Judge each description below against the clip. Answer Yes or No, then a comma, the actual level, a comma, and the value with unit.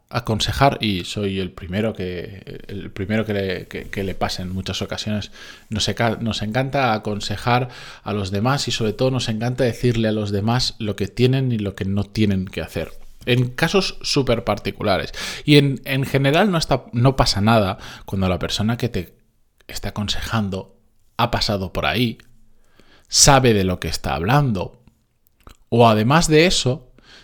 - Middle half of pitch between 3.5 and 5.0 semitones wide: Yes, average, 3.9 semitones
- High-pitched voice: No, low, 110 Hz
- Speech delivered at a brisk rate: No, average, 165 wpm